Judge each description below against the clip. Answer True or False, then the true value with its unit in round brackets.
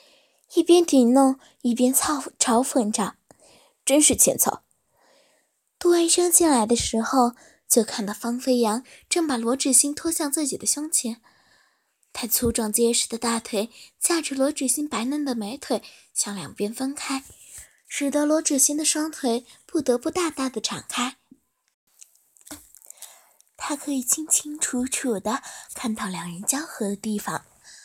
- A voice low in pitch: False (265 Hz)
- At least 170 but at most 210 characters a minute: True (205 characters per minute)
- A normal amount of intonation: True (4.2 semitones)